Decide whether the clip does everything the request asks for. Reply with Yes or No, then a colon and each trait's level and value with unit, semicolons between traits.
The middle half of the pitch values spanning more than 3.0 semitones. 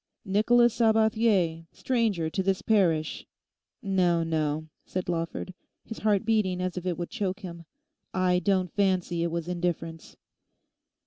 Yes: average, 3.4 semitones